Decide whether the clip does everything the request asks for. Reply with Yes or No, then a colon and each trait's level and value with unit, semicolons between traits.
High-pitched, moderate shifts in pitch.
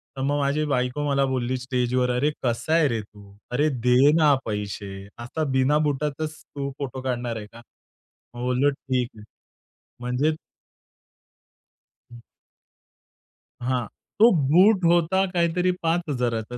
No: low, 130 Hz; average, 3.6 semitones